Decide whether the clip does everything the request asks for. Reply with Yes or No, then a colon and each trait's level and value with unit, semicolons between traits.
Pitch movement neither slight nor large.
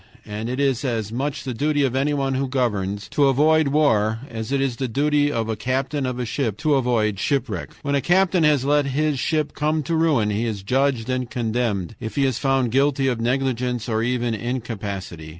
Yes: average, 3.8 semitones